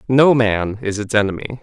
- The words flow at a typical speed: Yes, average, 185 wpm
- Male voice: Yes, male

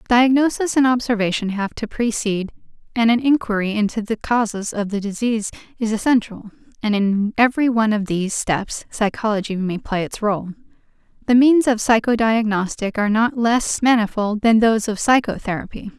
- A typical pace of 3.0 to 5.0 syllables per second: No, 5.4 syllables/s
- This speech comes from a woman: Yes, female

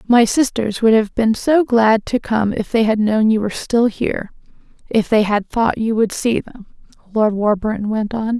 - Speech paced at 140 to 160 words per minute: No, average, 200 wpm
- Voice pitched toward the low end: No, high, 220 Hz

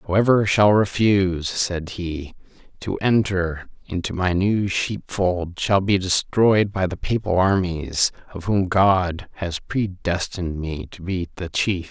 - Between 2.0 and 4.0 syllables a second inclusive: Yes, 3.7 syllables/s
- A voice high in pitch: No, very low, 95 Hz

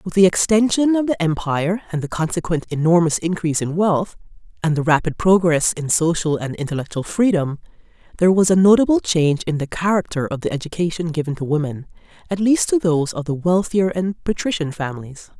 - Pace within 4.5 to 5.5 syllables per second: No, 5.9 syllables/s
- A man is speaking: No, female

